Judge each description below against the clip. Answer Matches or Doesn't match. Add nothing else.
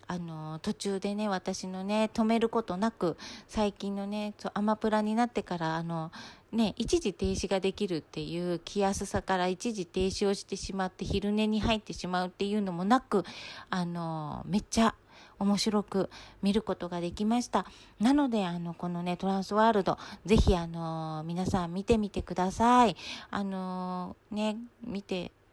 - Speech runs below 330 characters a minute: Matches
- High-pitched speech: Matches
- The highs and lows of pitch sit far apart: Doesn't match